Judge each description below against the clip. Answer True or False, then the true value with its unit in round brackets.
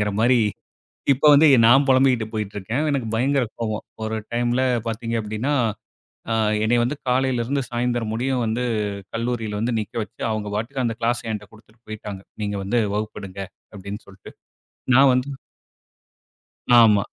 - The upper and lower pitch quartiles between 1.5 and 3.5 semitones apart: True (2.7 semitones)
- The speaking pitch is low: True (115 Hz)